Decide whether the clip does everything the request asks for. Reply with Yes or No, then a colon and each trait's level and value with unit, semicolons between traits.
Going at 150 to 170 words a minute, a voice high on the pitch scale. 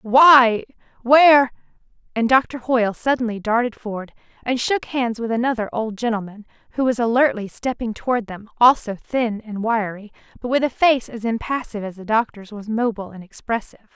Yes: average, 160 wpm; high, 230 Hz